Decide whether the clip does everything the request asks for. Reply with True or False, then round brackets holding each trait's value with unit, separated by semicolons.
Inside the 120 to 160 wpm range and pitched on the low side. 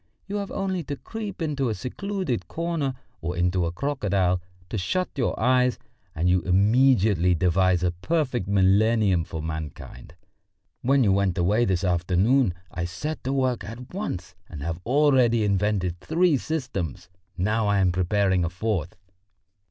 True (150 wpm; 100 Hz)